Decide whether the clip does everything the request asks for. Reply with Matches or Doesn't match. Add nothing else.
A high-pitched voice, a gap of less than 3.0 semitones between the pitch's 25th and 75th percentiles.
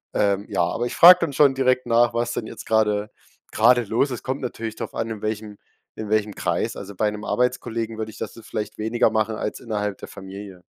Doesn't match